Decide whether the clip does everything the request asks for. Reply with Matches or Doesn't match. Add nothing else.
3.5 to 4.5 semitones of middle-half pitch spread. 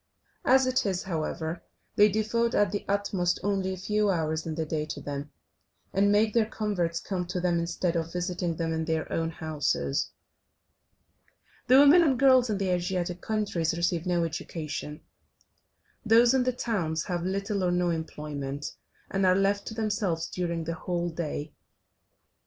Matches